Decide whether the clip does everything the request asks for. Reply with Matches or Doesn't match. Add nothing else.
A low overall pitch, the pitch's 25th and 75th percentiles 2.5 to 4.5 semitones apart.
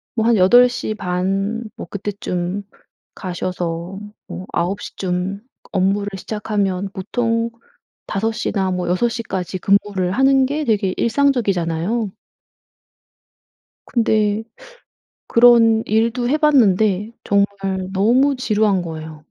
Doesn't match